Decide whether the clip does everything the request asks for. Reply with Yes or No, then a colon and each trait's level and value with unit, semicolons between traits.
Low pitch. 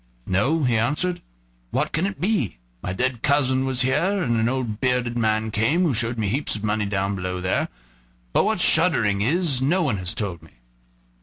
Yes: low, 120 Hz